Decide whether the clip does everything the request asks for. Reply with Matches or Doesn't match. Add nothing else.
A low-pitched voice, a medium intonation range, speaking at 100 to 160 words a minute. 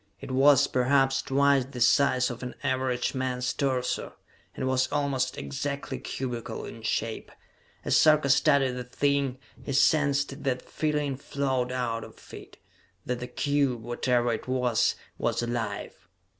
Doesn't match